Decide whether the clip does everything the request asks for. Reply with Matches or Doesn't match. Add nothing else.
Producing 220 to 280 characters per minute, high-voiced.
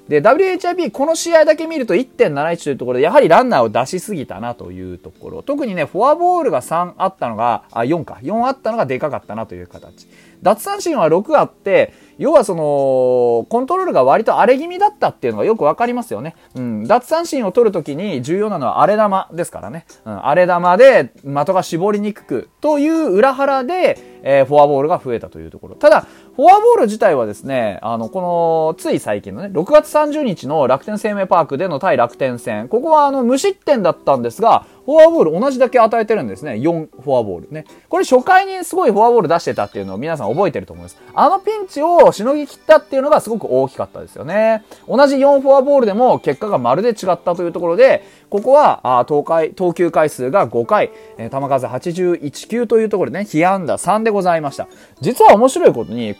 Doesn't match